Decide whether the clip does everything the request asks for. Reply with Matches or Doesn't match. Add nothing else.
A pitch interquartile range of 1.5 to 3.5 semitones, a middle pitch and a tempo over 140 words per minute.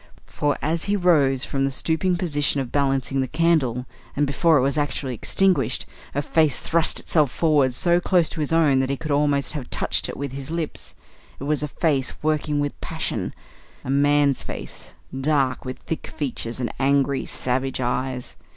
Matches